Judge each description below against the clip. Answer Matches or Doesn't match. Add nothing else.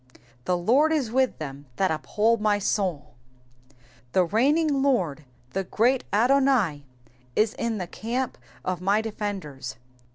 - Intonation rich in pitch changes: Matches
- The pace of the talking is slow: Matches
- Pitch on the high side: Matches